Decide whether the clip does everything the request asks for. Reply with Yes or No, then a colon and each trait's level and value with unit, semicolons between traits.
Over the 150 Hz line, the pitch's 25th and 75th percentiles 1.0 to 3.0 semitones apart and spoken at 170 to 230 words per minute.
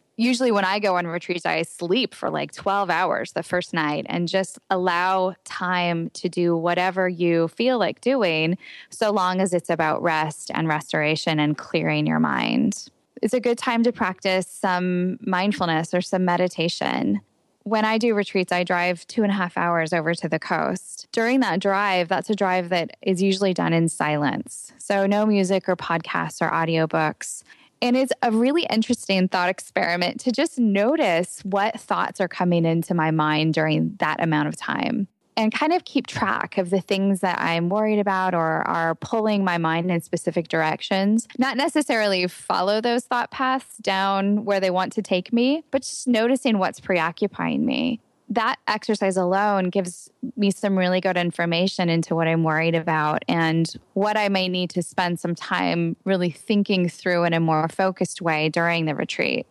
No: medium, 185 Hz; average, 3.8 semitones; average, 180 wpm